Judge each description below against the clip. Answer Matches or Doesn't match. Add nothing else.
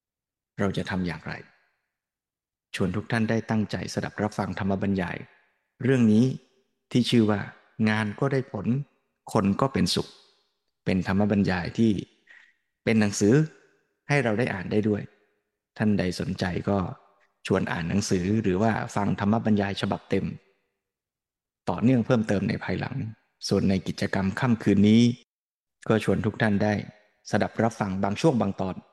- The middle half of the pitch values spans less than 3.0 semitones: Matches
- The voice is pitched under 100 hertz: Doesn't match